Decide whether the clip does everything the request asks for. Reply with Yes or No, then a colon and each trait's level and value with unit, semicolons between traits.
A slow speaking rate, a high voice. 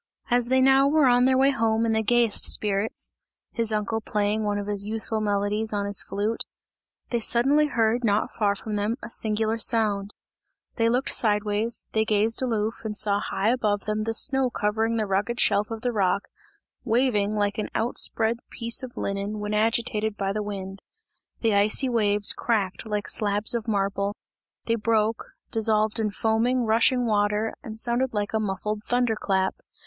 No: average, 175 wpm; high, 220 Hz